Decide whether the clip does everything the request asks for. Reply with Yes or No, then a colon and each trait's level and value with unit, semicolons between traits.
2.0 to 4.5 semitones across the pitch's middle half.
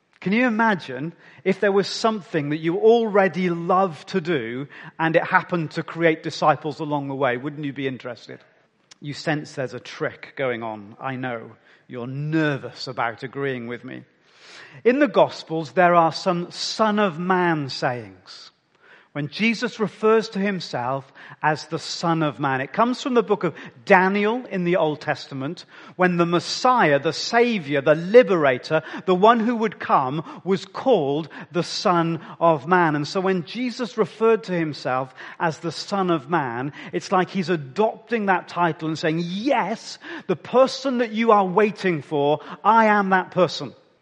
No: average, 5.2 semitones